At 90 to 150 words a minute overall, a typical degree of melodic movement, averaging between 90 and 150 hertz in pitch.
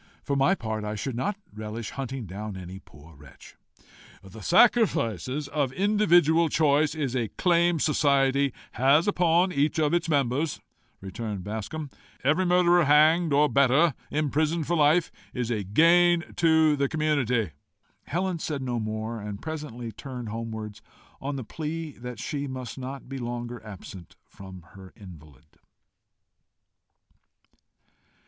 No: slow, 135 wpm; wide, 6.2 semitones; medium, 140 Hz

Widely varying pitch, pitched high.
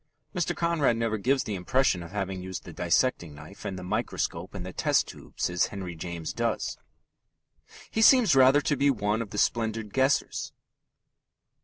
No: wide, 6.7 semitones; low, 105 Hz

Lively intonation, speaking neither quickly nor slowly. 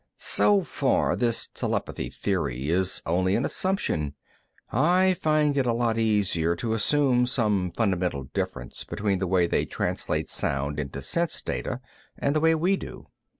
Yes: wide, 8.9 semitones; average, 150 wpm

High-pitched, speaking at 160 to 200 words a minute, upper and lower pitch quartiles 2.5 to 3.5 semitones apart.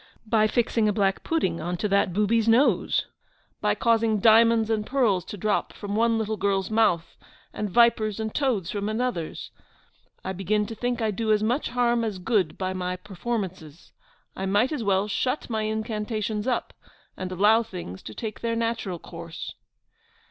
Yes: high, 215 Hz; average, 170 wpm; average, 3.1 semitones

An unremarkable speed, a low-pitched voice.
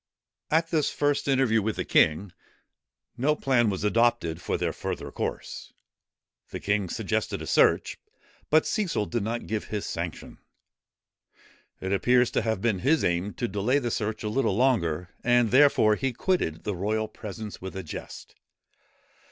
Yes: average, 160 wpm; low, 110 Hz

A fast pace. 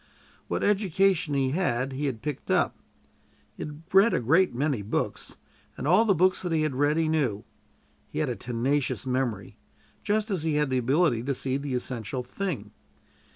No: average, 185 wpm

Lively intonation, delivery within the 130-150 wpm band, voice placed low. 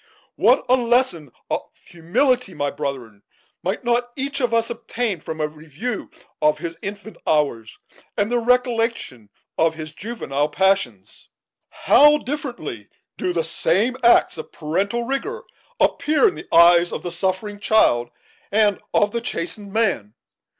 No: wide, 7.1 semitones; average, 145 wpm; high, 200 Hz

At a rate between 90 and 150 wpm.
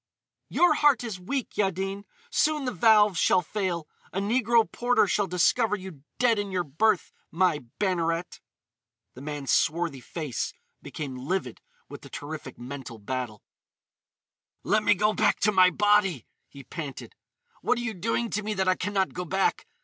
No: average, 165 wpm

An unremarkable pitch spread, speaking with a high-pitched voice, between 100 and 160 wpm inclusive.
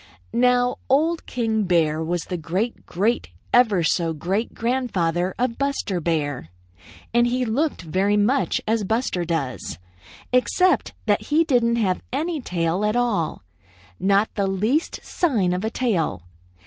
No: wide, 5.9 semitones; high, 210 Hz; average, 140 wpm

